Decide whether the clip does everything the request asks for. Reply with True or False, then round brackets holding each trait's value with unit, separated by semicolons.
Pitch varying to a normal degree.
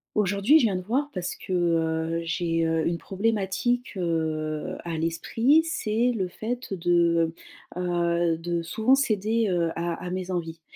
True (4.5 semitones)